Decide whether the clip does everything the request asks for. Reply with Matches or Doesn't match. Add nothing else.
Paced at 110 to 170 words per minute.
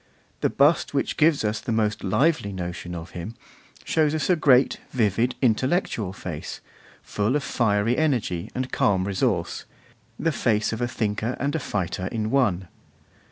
Matches